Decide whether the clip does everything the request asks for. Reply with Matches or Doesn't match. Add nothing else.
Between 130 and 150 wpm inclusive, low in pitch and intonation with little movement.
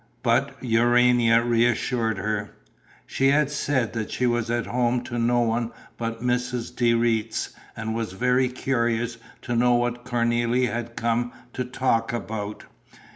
Matches